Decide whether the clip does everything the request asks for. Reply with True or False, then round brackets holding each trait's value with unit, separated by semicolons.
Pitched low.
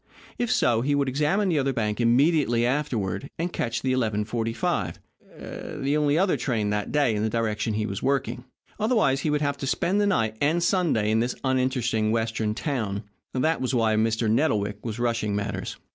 True (120 Hz)